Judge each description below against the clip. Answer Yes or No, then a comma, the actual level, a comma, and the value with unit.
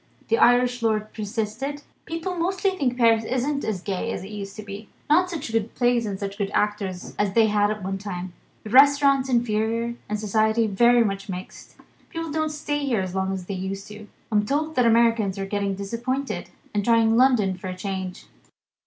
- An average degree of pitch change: Yes, average, 4.2 semitones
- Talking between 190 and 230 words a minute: Yes, average, 195 wpm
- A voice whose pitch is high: Yes, high, 220 Hz